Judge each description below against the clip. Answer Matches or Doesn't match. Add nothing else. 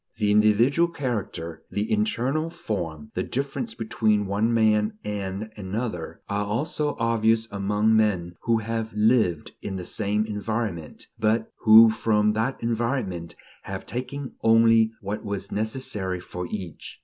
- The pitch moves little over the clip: Matches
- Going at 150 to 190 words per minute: Doesn't match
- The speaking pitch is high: Doesn't match